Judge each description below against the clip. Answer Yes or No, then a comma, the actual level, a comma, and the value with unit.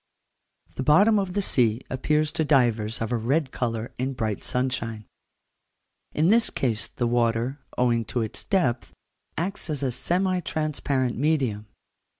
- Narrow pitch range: No, average, 4.9 semitones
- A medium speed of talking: Yes, average, 150 wpm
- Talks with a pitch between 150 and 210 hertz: No, low, 130 Hz